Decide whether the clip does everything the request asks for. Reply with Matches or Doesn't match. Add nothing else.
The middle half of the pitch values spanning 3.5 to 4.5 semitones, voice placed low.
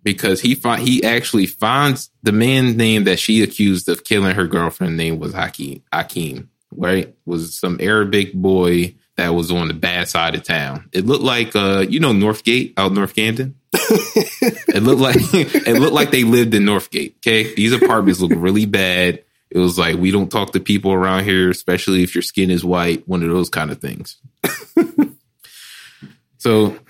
Matches